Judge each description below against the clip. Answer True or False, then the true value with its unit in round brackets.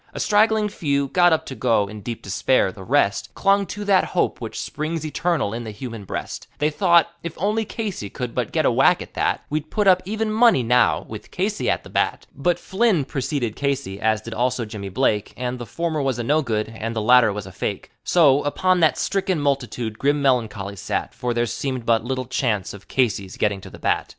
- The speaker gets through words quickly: True (220 wpm)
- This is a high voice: False (130 Hz)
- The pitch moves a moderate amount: False (7.3 semitones)